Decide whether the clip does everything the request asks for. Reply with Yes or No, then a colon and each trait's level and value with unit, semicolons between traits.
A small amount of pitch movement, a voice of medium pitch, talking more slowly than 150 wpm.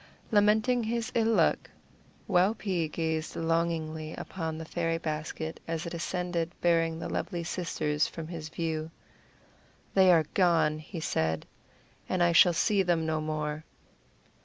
Yes: narrow, 2.1 semitones; medium, 165 Hz; slow, 135 wpm